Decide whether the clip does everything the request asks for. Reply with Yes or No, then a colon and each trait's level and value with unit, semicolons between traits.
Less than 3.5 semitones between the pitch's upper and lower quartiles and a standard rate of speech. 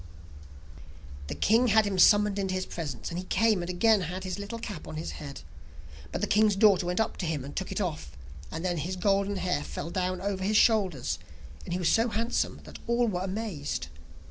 No: average, 3.1 semitones; fast, 215 wpm